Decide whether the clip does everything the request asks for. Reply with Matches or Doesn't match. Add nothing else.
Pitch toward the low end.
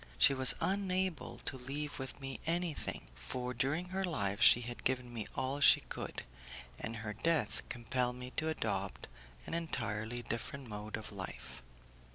Matches